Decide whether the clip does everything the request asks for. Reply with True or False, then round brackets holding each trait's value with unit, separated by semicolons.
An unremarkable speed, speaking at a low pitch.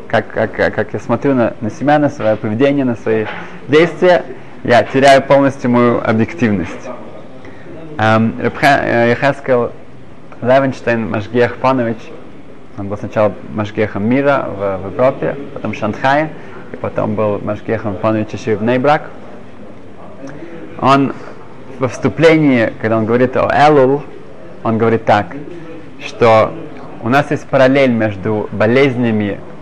True (125 wpm; 120 Hz)